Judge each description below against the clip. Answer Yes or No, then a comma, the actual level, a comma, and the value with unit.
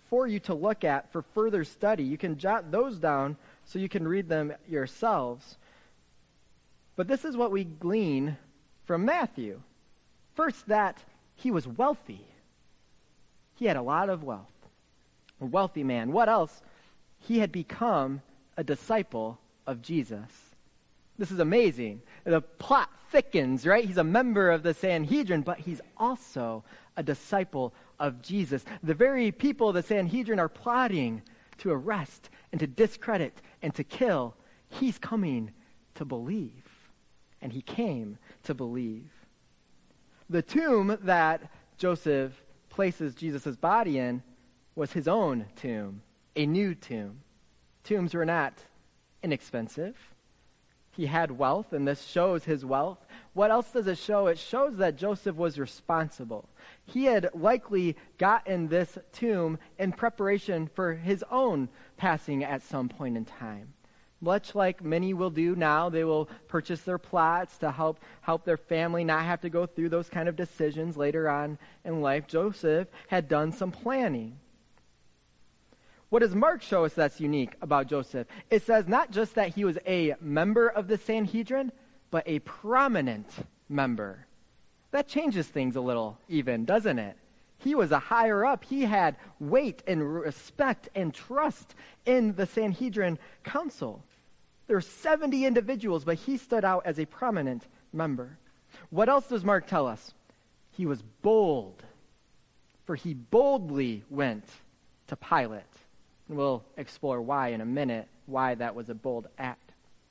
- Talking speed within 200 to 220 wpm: No, average, 150 wpm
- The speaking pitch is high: No, medium, 165 Hz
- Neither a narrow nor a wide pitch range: No, wide, 7.2 semitones